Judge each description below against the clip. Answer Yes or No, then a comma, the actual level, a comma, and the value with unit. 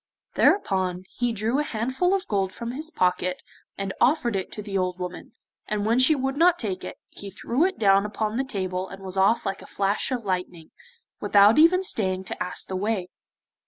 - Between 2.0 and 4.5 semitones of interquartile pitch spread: No, average, 5.3 semitones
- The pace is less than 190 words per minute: No, average, 200 wpm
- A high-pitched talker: Yes, high, 205 Hz